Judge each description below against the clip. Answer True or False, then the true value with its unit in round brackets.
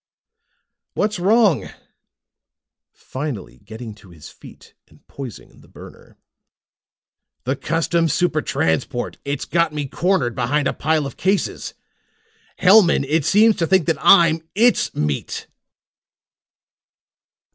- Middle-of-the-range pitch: True (155 Hz)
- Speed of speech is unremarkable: False (120 wpm)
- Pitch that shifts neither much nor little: False (6.1 semitones)